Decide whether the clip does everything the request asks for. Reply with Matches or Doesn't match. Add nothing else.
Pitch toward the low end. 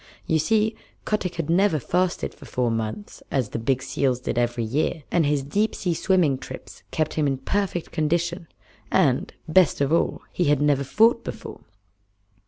Doesn't match